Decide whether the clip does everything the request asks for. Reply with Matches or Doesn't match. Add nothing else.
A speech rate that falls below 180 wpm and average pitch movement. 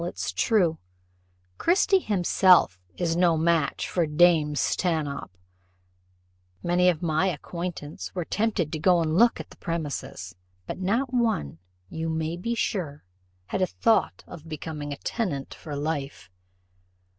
Matches